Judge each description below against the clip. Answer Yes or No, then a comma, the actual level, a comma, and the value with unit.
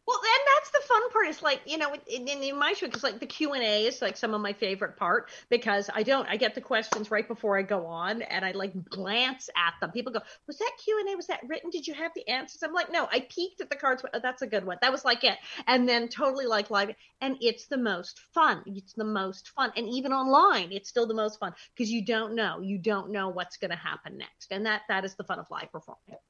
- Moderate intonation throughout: No, wide, 6.2 semitones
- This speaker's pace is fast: Yes, fast, 265 wpm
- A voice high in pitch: Yes, high, 235 Hz